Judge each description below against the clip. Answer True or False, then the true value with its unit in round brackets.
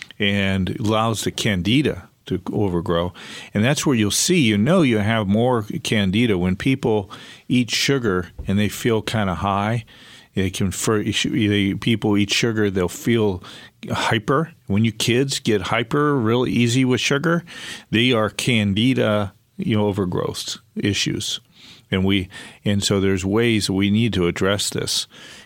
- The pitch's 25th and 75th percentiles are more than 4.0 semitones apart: False (3.7 semitones)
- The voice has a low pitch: True (105 Hz)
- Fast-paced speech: False (145 wpm)